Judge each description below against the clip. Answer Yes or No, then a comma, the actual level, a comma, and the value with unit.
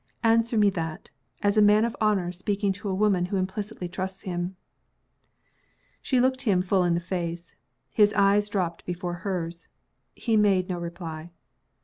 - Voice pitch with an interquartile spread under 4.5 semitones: Yes, average, 3.0 semitones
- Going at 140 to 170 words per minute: Yes, average, 160 wpm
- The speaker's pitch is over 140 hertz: Yes, high, 190 Hz